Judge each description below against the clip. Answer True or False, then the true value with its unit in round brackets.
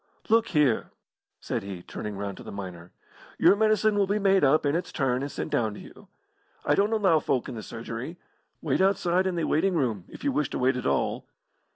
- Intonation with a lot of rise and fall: True (9.0 semitones)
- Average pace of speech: False (220 wpm)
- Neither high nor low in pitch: True (150 Hz)